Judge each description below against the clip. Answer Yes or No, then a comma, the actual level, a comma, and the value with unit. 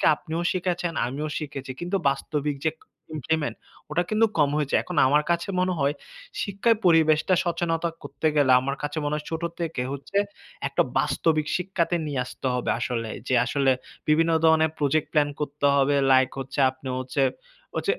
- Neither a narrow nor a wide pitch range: Yes, average, 3.3 semitones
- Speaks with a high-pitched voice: No, medium, 150 Hz